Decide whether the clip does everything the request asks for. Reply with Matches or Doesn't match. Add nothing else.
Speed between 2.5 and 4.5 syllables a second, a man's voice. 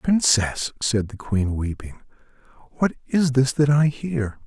Matches